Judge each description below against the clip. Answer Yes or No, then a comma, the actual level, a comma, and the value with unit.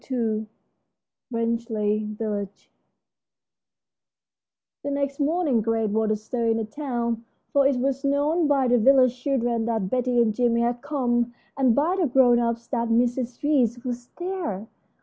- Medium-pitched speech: No, high, 240 Hz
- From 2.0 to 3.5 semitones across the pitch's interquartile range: Yes, average, 3.2 semitones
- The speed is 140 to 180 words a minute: Yes, average, 150 wpm